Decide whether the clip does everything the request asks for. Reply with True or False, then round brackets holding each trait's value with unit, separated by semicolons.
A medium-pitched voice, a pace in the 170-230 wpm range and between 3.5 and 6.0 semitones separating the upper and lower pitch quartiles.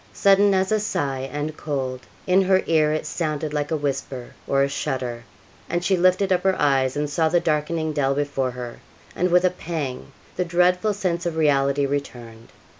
True (150 Hz; 190 wpm; 4.6 semitones)